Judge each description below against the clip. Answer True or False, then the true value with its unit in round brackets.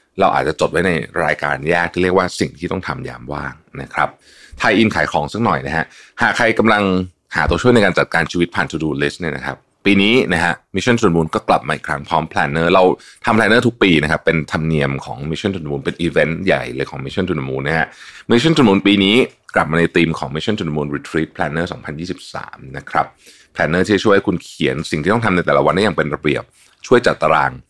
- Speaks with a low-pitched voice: True (85 Hz)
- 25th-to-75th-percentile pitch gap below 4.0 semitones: False (4.3 semitones)